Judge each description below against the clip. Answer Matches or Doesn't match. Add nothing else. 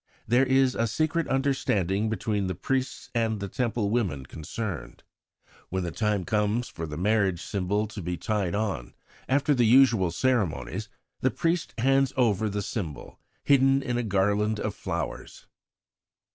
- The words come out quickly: Doesn't match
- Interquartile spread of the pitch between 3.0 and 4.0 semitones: Doesn't match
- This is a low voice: Matches